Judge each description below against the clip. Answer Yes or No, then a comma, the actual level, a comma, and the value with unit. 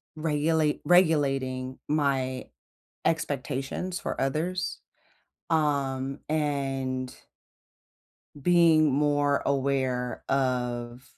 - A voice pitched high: No, medium, 140 Hz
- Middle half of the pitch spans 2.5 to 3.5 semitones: Yes, average, 2.9 semitones